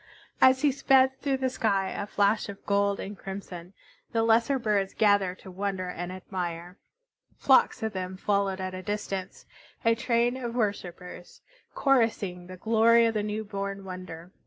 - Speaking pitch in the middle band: No, high, 200 Hz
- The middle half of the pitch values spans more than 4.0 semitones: No, average, 3.5 semitones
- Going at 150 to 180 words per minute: Yes, average, 160 wpm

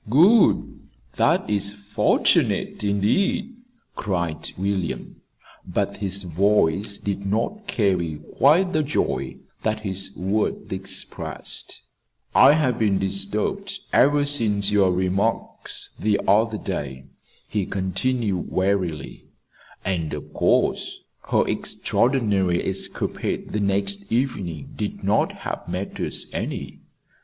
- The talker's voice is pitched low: Yes, low, 100 Hz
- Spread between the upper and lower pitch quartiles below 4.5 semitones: Yes, average, 3.3 semitones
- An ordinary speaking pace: No, slow, 105 wpm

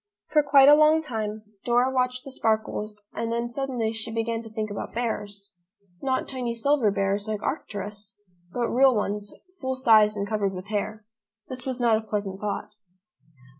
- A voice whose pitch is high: Yes, high, 225 Hz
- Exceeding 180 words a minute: No, average, 170 wpm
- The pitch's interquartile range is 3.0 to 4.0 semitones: Yes, average, 3.3 semitones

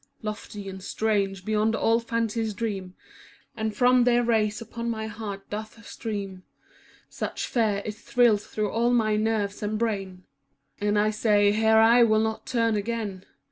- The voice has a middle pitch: No, high, 215 Hz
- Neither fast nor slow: Yes, average, 160 wpm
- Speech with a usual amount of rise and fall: No, narrow, 1.8 semitones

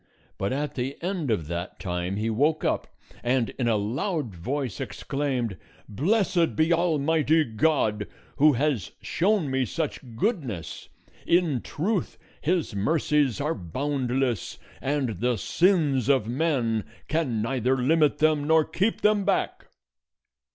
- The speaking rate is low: Yes, slow, 130 wpm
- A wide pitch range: Yes, wide, 5.7 semitones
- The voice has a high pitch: No, medium, 140 Hz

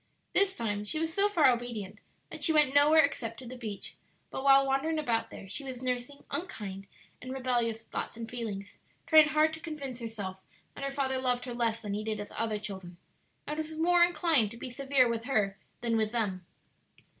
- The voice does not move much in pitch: No, average, 4.8 semitones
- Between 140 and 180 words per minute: No, average, 200 wpm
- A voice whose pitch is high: Yes, high, 245 Hz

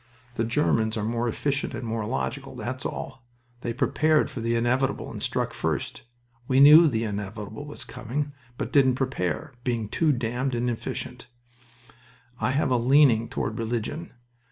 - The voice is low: Yes, low, 125 Hz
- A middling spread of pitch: Yes, average, 3.3 semitones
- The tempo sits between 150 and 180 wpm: Yes, average, 155 wpm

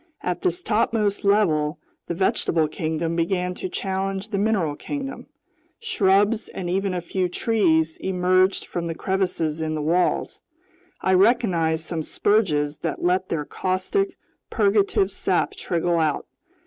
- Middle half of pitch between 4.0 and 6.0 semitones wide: No, average, 3.5 semitones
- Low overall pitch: No, medium, 185 Hz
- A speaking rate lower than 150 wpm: Yes, slow, 135 wpm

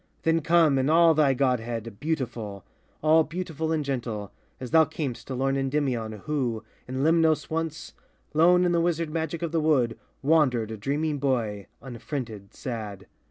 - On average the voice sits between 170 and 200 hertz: No, medium, 140 Hz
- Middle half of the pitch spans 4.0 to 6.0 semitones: Yes, average, 5.3 semitones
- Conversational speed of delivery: Yes, average, 160 wpm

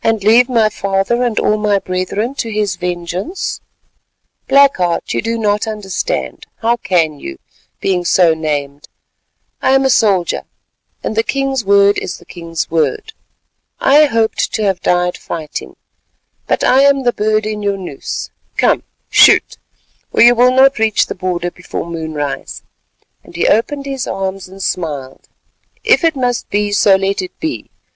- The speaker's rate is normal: Yes, average, 160 wpm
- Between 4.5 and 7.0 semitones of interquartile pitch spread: Yes, average, 5.1 semitones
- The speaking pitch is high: Yes, high, 205 Hz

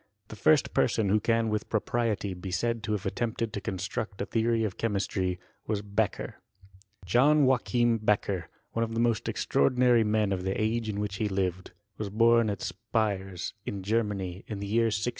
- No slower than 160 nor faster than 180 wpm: No, average, 190 wpm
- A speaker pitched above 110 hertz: No, low, 105 Hz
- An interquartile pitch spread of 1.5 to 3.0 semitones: Yes, average, 2.7 semitones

